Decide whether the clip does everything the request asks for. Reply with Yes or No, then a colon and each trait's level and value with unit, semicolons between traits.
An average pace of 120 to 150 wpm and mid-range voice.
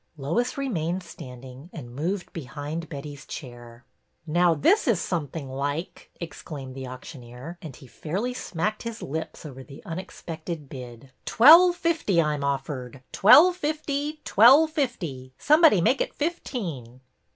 Yes: average, 145 wpm; medium, 160 Hz